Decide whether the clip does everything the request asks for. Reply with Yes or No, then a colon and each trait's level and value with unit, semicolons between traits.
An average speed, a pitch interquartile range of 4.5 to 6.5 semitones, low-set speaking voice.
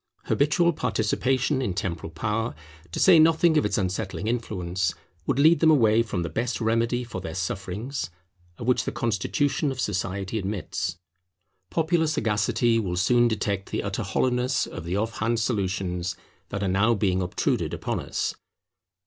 Yes: average, 155 wpm; average, 4.9 semitones; low, 110 Hz